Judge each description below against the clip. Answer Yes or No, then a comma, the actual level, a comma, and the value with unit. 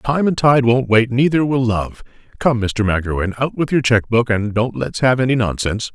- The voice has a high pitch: No, low, 120 Hz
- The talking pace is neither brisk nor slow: No, fast, 230 wpm